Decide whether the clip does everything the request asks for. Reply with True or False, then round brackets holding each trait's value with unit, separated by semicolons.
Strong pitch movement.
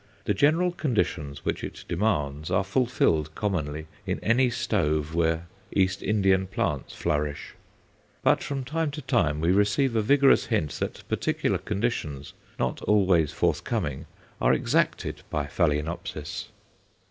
True (7.5 semitones)